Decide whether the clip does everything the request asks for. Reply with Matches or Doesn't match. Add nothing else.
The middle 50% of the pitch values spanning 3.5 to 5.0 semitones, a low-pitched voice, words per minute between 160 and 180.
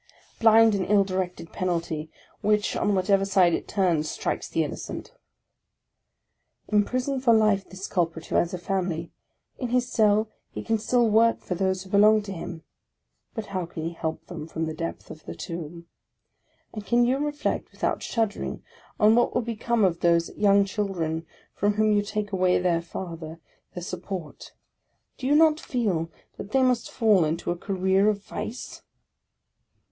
Doesn't match